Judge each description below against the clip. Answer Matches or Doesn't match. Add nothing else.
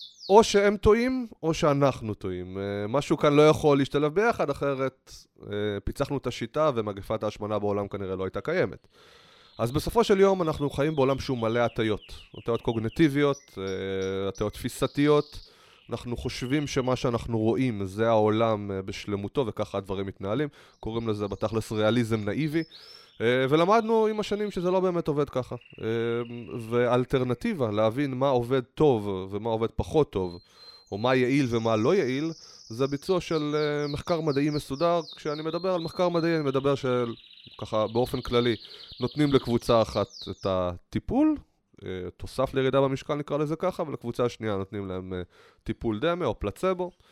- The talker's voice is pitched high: Doesn't match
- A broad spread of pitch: Matches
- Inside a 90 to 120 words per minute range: Doesn't match